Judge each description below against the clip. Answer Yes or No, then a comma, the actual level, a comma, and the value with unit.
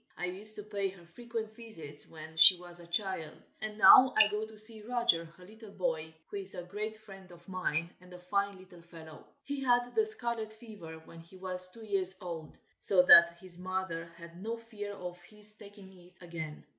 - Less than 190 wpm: No, fast, 205 wpm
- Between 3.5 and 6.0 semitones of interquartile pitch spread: Yes, average, 3.9 semitones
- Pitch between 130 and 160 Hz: No, high, 190 Hz